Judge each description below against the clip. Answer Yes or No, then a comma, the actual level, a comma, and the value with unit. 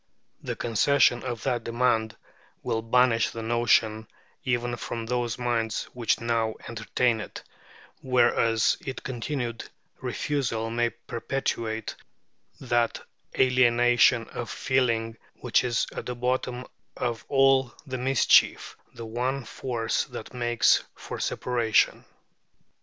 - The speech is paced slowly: Yes, slow, 115 wpm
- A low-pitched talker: Yes, low, 120 Hz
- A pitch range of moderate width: No, narrow, 1.7 semitones